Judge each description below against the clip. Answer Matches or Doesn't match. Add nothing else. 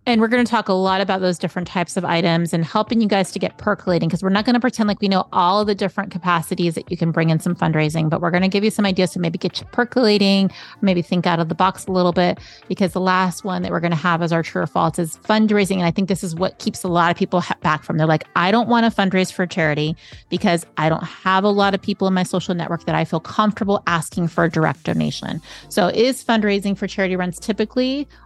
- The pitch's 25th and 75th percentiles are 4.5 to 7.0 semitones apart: Doesn't match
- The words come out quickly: Matches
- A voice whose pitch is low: Doesn't match